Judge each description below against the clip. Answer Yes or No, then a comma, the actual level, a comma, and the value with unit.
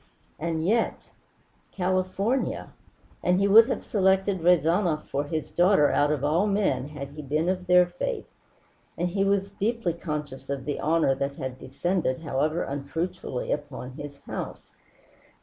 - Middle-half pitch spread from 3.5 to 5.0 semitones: Yes, average, 4.7 semitones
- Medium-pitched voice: Yes, medium, 165 Hz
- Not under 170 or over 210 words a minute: No, average, 150 wpm